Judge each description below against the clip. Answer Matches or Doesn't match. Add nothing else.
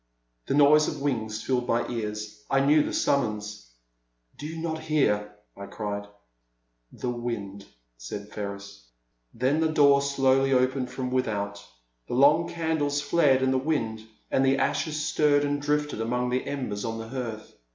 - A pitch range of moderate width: Matches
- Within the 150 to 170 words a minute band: Matches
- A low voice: Matches